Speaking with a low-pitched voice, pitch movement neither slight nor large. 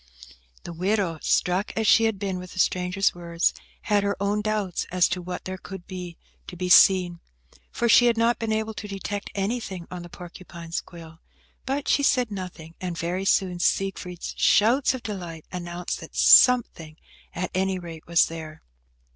No: medium, 185 Hz; average, 3.1 semitones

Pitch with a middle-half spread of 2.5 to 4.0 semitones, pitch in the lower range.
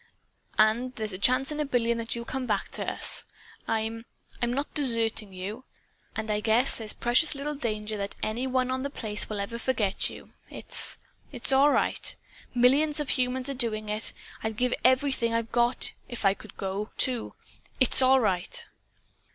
No: average, 3.1 semitones; high, 235 Hz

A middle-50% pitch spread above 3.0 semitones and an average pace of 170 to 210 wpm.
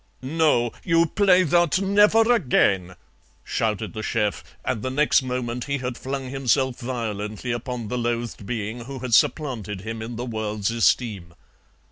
No: average, 3.9 semitones; average, 150 wpm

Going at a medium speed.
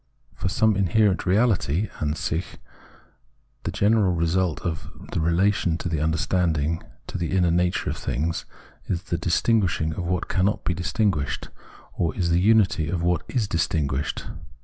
Yes: average, 150 wpm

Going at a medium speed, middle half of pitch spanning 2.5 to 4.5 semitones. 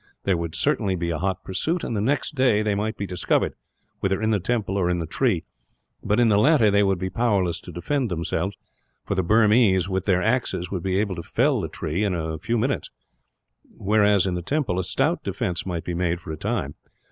No: fast, 220 wpm; average, 3.7 semitones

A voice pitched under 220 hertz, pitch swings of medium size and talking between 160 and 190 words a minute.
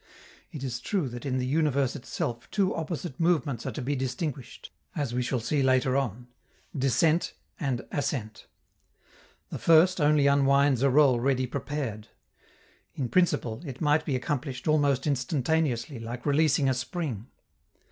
No: low, 135 Hz; average, 3.2 semitones; average, 145 wpm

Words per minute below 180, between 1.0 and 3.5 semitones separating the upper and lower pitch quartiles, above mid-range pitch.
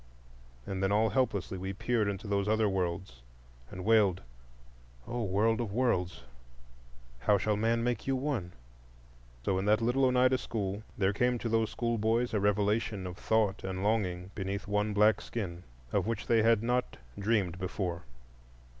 No: average, 160 wpm; average, 3.2 semitones; low, 105 Hz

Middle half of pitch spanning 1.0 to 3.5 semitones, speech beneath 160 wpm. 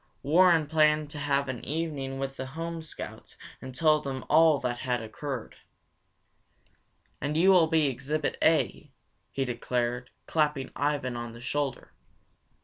Yes: average, 3.1 semitones; average, 140 wpm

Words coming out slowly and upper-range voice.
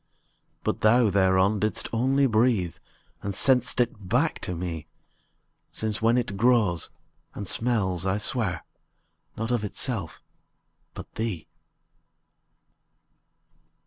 No: slow, 105 wpm; low, 105 Hz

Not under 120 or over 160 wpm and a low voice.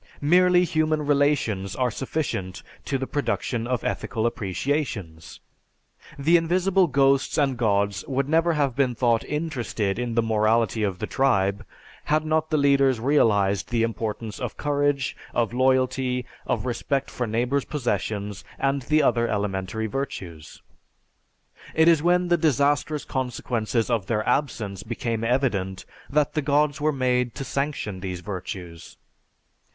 Yes: average, 140 wpm; low, 125 Hz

